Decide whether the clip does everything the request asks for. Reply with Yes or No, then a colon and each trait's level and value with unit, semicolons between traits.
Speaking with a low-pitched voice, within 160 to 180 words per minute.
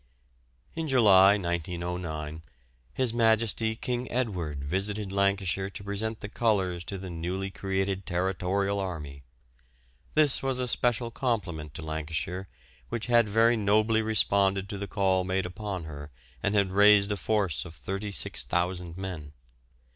No: very low, 95 Hz; slow, 135 wpm